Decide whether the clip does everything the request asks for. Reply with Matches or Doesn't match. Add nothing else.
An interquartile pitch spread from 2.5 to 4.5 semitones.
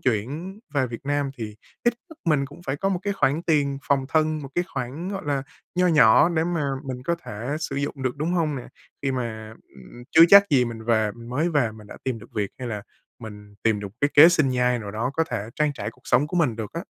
Doesn't match